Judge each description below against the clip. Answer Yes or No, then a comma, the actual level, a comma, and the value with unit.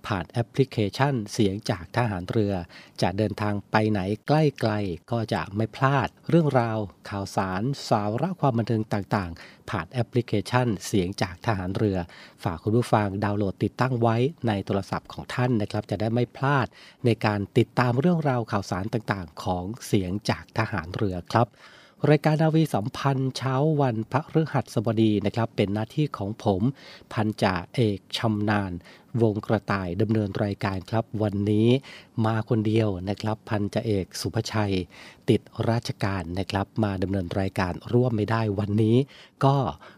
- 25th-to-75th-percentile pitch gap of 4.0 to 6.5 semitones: No, average, 3.4 semitones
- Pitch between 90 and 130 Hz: Yes, low, 110 Hz